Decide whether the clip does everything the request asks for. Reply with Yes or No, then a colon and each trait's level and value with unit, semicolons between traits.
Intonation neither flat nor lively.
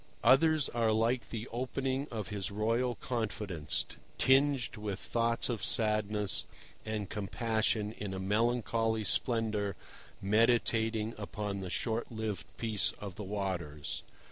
No: narrow, 2.3 semitones